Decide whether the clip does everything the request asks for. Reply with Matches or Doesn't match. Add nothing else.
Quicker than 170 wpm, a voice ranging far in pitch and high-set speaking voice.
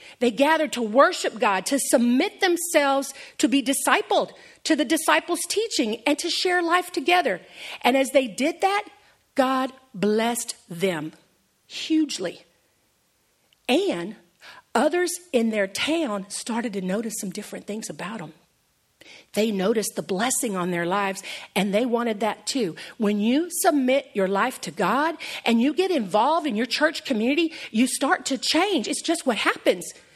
Doesn't match